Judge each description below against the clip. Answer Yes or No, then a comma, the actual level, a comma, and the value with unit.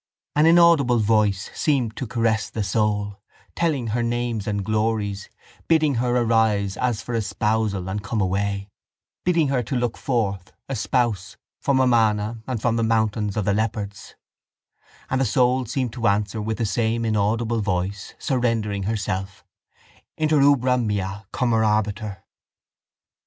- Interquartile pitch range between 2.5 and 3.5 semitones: Yes, average, 3.0 semitones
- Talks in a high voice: No, low, 110 Hz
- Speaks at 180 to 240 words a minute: No, average, 140 wpm